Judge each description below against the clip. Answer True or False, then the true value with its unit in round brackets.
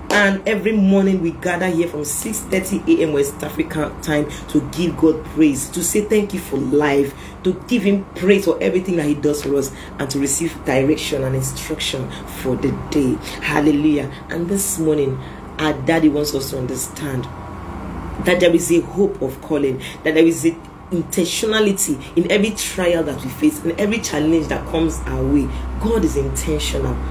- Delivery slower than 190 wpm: True (180 wpm)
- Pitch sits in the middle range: True (155 Hz)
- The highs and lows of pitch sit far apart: False (4.2 semitones)